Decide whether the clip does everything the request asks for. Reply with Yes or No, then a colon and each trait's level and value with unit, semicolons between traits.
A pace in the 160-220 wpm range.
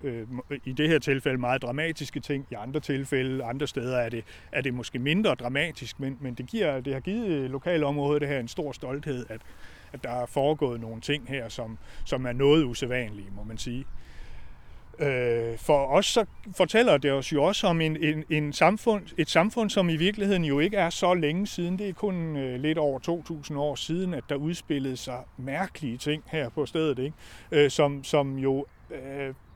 Yes: average, 190 wpm